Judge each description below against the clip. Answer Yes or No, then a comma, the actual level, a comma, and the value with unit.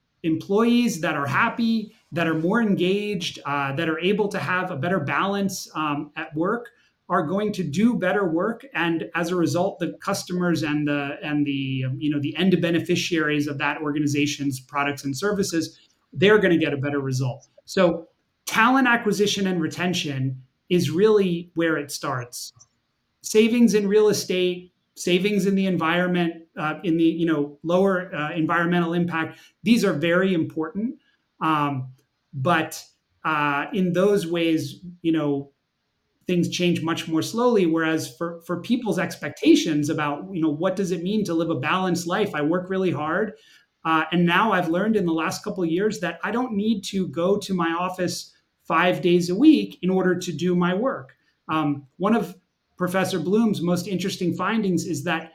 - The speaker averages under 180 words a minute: Yes, average, 170 wpm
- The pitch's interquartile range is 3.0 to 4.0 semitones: Yes, average, 3.6 semitones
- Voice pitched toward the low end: No, medium, 175 Hz